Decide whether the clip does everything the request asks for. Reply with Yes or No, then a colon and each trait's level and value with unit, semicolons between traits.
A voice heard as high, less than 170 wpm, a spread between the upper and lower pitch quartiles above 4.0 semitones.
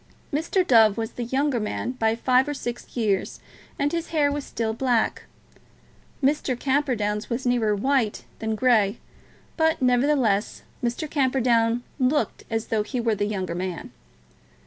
No: high, 240 Hz; average, 145 wpm; average, 3.6 semitones